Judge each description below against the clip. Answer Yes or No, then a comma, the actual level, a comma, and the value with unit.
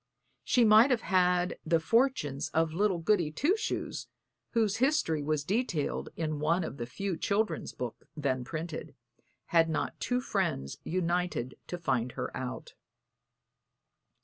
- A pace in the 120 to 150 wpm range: Yes, average, 140 wpm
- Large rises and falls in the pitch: Yes, wide, 5.7 semitones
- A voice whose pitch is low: No, medium, 170 Hz